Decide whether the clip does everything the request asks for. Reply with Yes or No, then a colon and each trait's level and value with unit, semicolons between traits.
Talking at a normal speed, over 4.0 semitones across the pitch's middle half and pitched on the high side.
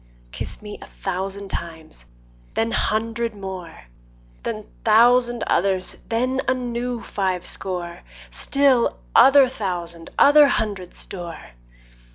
No: slow, 110 wpm; average, 5.1 semitones; high, 205 Hz